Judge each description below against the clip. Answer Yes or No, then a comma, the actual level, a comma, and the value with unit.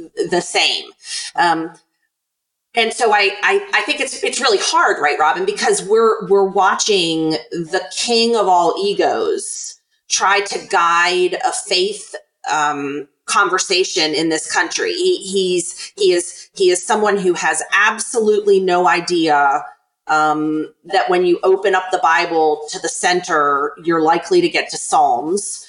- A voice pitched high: Yes, high, 225 Hz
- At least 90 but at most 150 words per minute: Yes, average, 145 wpm